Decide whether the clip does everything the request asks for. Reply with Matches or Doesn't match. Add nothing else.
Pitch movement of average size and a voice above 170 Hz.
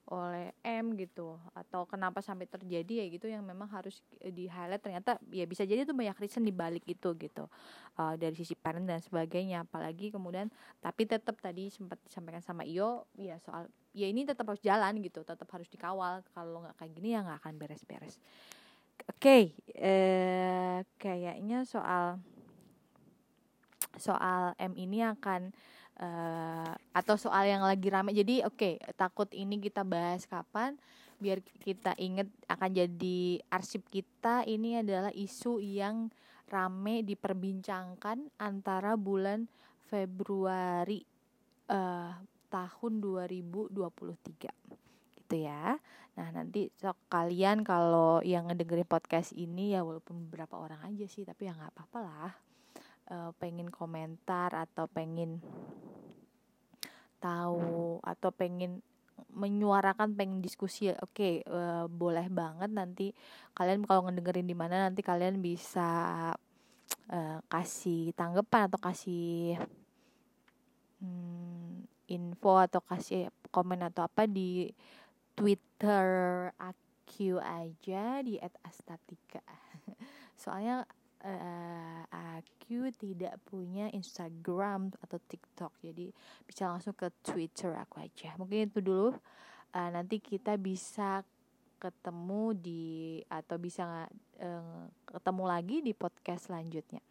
Matches